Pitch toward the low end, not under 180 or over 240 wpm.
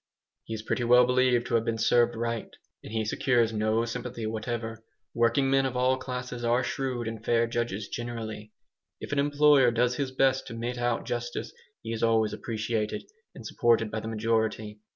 Yes: low, 115 Hz; average, 185 wpm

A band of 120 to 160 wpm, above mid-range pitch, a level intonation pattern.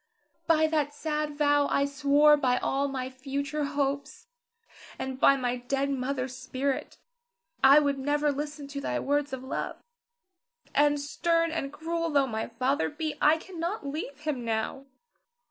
Yes: average, 150 wpm; very high, 285 Hz; narrow, 1.9 semitones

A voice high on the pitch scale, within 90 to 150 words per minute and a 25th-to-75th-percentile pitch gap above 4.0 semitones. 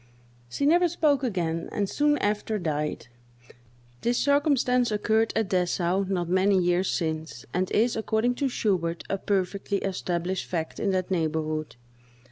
Yes: high, 195 Hz; average, 140 wpm; average, 4.7 semitones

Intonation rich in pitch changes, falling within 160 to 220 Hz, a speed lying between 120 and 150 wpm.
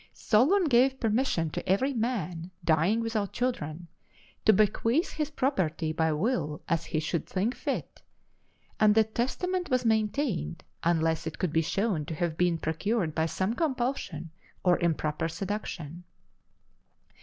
Yes: wide, 6.7 semitones; high, 190 Hz; average, 140 wpm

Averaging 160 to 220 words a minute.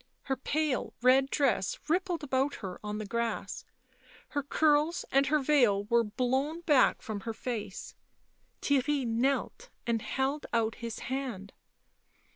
No: slow, 135 wpm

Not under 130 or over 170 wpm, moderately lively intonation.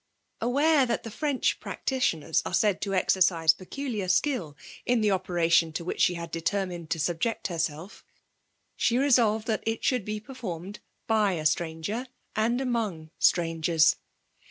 No: average, 145 wpm; wide, 5.8 semitones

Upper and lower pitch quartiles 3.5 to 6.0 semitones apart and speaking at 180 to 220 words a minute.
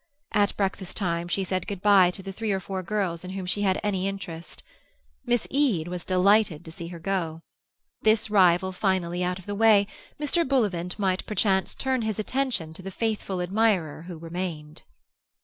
No: average, 2.9 semitones; average, 185 wpm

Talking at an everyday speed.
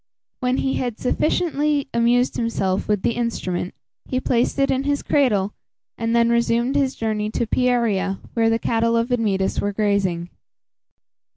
Yes: average, 155 wpm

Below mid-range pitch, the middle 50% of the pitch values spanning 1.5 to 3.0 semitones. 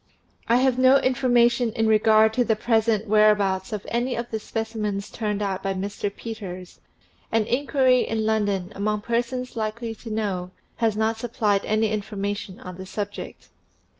No: high, 220 Hz; narrow, 2.5 semitones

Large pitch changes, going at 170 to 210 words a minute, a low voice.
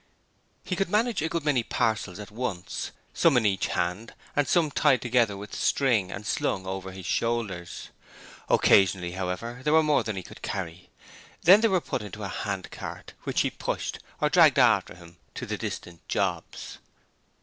Yes: wide, 7.1 semitones; average, 175 wpm; low, 105 Hz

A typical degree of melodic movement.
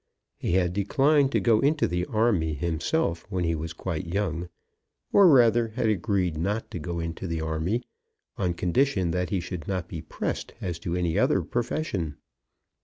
Yes: average, 5.0 semitones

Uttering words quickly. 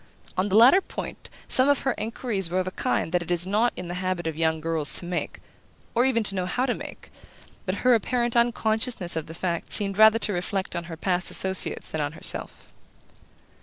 Yes: fast, 215 wpm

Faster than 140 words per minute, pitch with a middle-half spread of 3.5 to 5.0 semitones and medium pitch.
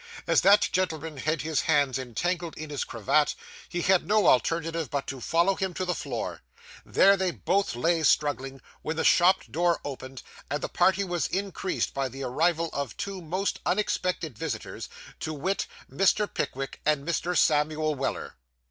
Yes: average, 165 wpm; average, 4.3 semitones; medium, 160 Hz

